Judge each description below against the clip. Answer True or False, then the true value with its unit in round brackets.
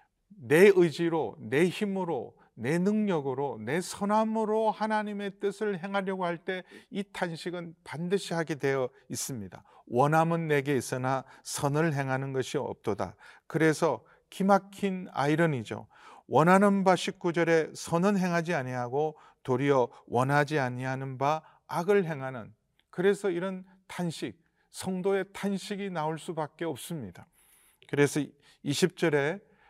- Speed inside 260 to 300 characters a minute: True (265 characters per minute)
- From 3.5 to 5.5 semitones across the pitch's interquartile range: True (5.2 semitones)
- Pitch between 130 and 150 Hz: False (170 Hz)